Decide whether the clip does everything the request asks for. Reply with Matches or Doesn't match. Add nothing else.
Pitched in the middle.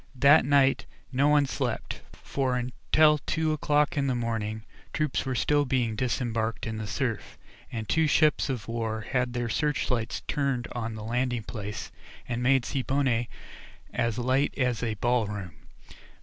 Doesn't match